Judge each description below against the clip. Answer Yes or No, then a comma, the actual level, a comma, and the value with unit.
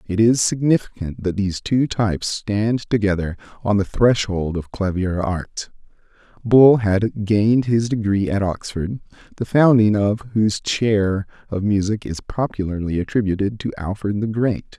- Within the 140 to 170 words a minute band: Yes, average, 145 wpm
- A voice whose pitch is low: Yes, low, 105 Hz